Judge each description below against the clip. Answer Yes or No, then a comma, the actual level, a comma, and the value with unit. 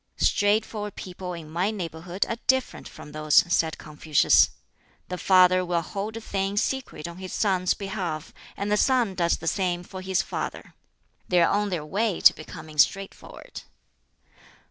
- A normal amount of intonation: Yes, average, 3.3 semitones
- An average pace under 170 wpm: Yes, average, 160 wpm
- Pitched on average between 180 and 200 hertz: Yes, medium, 185 Hz